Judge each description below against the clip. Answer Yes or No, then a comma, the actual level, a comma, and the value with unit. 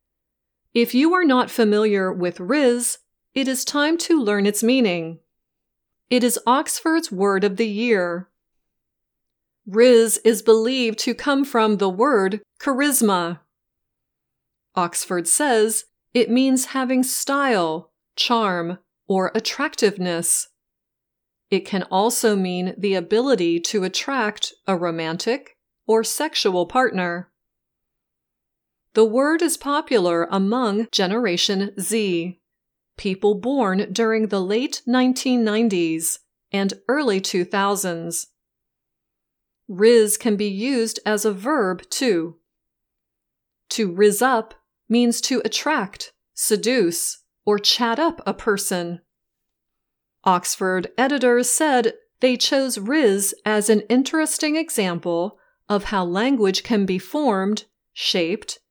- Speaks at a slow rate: Yes, slow, 105 wpm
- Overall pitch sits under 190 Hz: No, high, 220 Hz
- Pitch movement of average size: Yes, average, 4.8 semitones